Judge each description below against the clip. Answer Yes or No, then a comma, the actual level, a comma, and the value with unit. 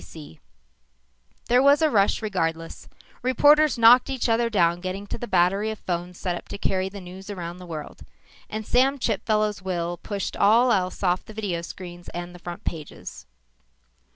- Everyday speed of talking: Yes, average, 180 wpm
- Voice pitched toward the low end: No, high, 195 Hz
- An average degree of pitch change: Yes, average, 4.4 semitones